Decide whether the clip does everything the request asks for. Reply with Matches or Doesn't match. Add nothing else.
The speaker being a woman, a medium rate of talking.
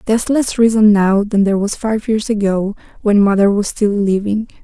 Matches